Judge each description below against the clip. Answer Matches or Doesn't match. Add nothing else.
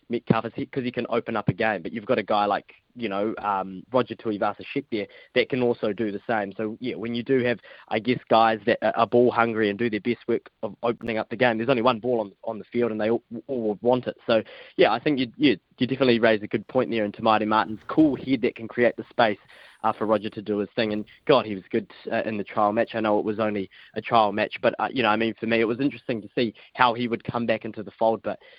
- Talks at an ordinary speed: Doesn't match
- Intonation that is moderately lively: Doesn't match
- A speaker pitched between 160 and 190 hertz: Doesn't match